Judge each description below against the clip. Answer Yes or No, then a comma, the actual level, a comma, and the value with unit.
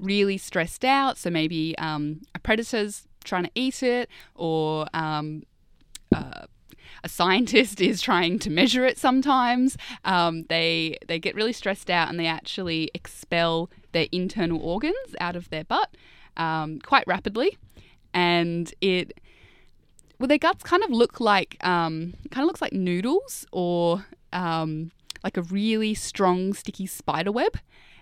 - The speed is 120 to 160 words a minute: Yes, average, 150 wpm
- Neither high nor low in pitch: Yes, medium, 180 Hz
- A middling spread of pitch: No, wide, 6.3 semitones